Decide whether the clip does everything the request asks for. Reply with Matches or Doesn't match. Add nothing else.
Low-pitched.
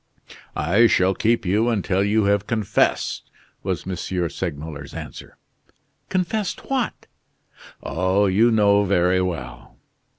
Matches